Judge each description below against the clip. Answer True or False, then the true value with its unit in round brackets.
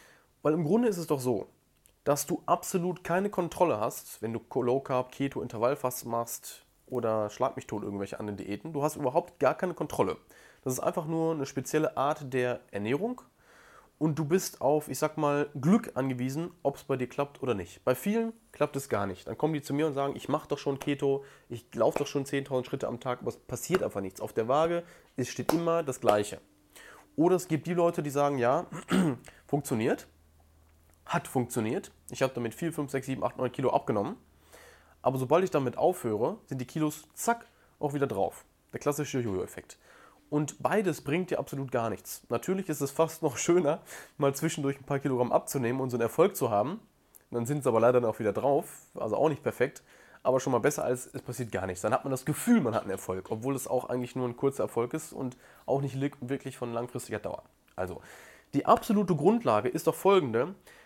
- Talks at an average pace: False (210 wpm)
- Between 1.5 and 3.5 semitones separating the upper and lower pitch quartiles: False (4.3 semitones)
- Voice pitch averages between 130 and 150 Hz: True (140 Hz)